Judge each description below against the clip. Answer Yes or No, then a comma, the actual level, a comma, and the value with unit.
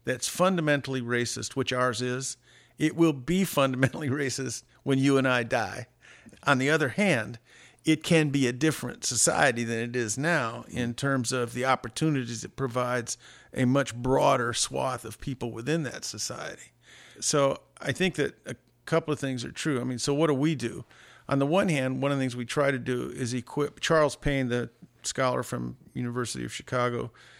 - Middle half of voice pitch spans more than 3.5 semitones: No, average, 3.0 semitones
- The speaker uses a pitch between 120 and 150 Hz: Yes, low, 135 Hz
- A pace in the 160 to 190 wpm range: Yes, average, 185 wpm